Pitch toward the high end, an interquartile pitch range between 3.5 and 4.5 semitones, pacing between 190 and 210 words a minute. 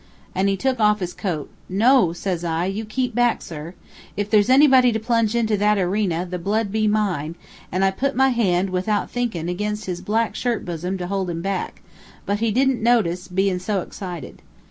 Yes: high, 200 Hz; average, 3.9 semitones; average, 195 wpm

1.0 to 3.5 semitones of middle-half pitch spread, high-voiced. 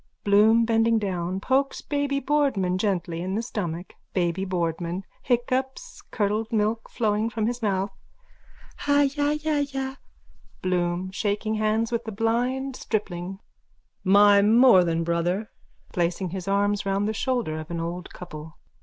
No: average, 4.6 semitones; high, 205 Hz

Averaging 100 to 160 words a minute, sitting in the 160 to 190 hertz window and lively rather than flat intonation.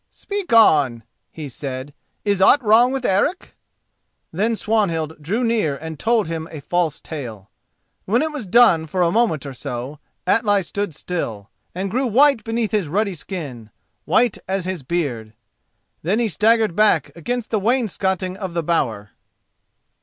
Yes: average, 155 wpm; medium, 185 Hz; wide, 6.5 semitones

